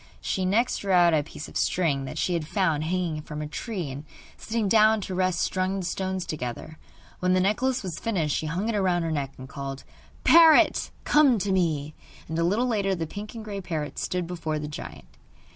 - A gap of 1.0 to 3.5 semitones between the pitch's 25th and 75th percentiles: No, average, 4.5 semitones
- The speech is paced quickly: Yes, fast, 210 wpm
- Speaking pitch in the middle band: Yes, medium, 180 Hz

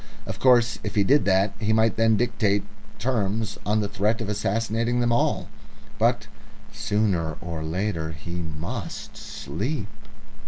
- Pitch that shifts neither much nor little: Yes, average, 3.1 semitones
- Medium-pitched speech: No, low, 105 Hz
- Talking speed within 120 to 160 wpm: Yes, average, 145 wpm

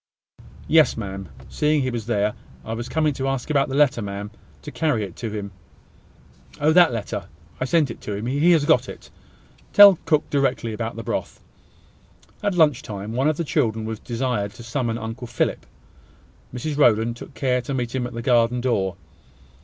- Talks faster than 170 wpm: Yes, average, 190 wpm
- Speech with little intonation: No, average, 4.3 semitones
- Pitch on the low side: Yes, low, 120 Hz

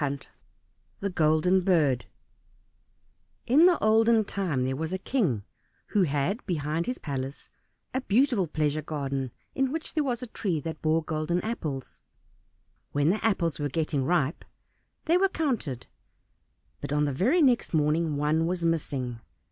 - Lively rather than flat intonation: Yes, wide, 6.8 semitones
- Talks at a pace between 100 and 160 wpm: Yes, average, 150 wpm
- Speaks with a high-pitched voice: No, medium, 165 Hz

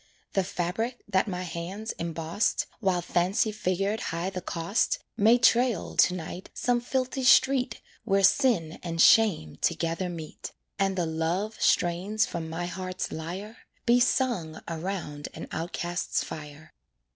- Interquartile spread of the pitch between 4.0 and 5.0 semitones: Yes, average, 4.5 semitones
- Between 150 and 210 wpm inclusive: No, slow, 135 wpm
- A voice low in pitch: No, medium, 185 Hz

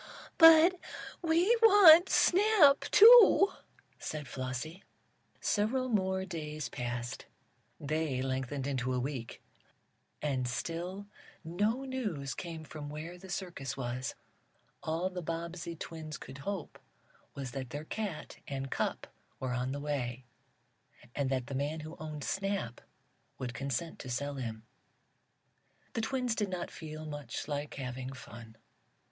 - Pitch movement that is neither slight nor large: No, wide, 6.6 semitones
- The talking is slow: Yes, slow, 130 wpm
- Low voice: No, medium, 155 Hz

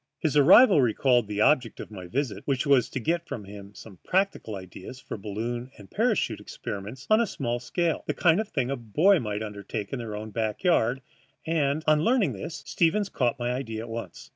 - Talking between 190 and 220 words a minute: Yes, average, 195 wpm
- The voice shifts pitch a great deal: Yes, wide, 6.4 semitones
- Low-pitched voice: Yes, low, 125 Hz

